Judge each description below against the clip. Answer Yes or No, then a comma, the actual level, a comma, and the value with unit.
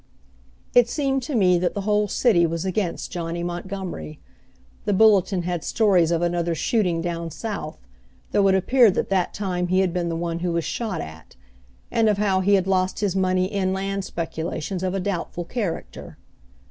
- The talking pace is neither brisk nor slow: Yes, average, 185 wpm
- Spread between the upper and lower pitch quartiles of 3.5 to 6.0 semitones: No, average, 2.8 semitones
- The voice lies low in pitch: No, medium, 185 Hz